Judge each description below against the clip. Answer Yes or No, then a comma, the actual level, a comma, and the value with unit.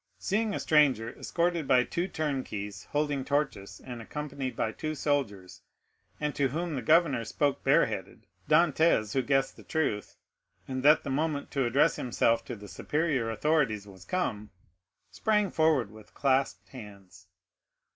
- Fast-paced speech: No, average, 145 wpm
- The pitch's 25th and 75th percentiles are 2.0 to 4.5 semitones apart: No, wide, 5.4 semitones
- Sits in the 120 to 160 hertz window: Yes, low, 135 Hz